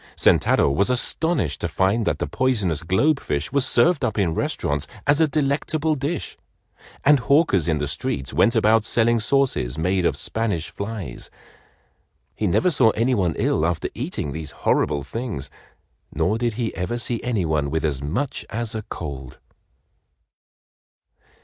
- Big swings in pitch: Yes, wide, 8.0 semitones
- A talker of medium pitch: No, low, 110 Hz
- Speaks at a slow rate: No, average, 155 wpm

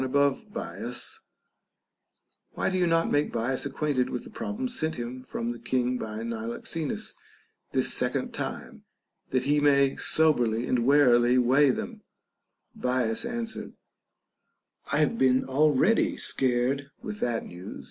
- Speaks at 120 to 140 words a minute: Yes, slow, 135 wpm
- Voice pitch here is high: No, low, 130 Hz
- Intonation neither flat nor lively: Yes, average, 3.9 semitones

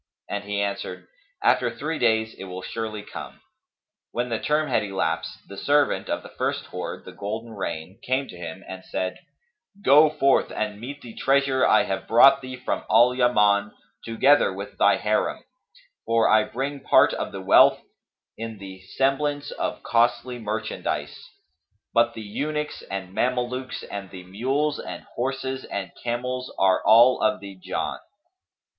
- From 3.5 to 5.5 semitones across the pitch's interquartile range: Yes, average, 4.7 semitones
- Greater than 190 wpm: No, average, 160 wpm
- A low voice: Yes, low, 115 Hz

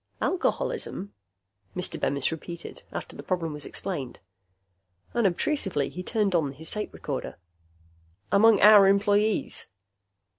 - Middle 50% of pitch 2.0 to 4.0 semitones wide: No, average, 4.4 semitones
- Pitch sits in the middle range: No, high, 195 Hz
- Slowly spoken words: Yes, slow, 110 wpm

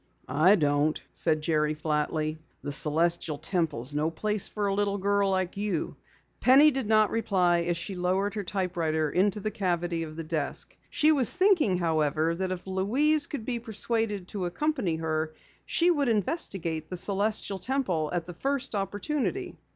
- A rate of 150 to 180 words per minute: Yes, average, 165 wpm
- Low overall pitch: No, medium, 185 Hz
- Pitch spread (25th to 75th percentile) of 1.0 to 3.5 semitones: No, average, 4.9 semitones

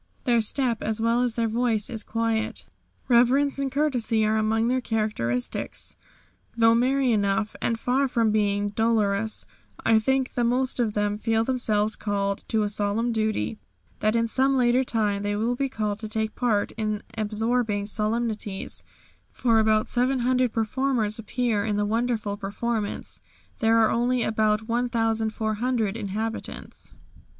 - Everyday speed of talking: Yes, average, 145 wpm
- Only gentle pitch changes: Yes, narrow, 2.2 semitones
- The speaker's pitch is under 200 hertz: No, high, 225 Hz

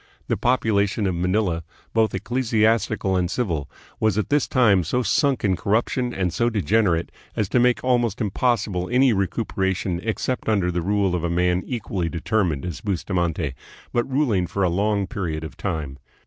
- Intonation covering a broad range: No, average, 4.4 semitones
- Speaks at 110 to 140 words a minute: No, average, 170 wpm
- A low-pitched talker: Yes, low, 100 Hz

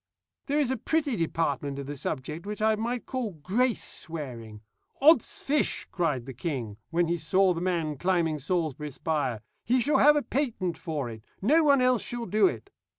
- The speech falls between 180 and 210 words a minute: Yes, average, 185 wpm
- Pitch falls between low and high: Yes, medium, 175 Hz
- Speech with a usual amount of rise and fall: No, wide, 8.5 semitones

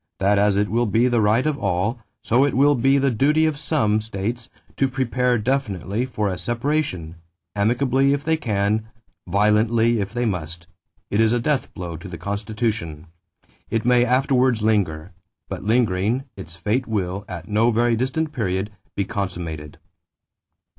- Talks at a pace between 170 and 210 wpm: No, average, 160 wpm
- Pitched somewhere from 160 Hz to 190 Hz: No, low, 110 Hz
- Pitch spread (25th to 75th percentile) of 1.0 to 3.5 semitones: No, average, 4.3 semitones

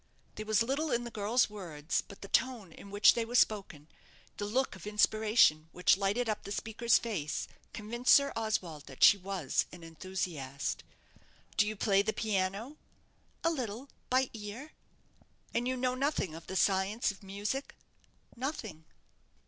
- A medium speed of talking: Yes, average, 160 wpm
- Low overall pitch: No, high, 210 Hz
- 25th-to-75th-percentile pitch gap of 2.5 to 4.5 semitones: Yes, average, 4.1 semitones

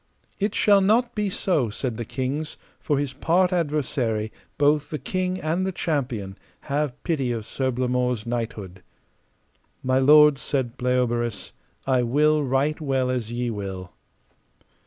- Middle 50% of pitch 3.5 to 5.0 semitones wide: Yes, average, 4.3 semitones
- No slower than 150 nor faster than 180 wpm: No, average, 140 wpm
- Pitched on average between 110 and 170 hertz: Yes, low, 135 Hz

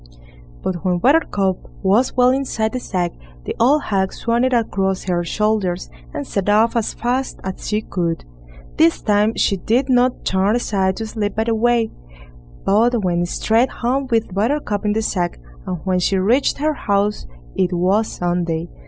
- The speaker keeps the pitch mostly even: No, average, 4.1 semitones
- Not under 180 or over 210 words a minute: No, average, 170 wpm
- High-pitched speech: Yes, high, 210 Hz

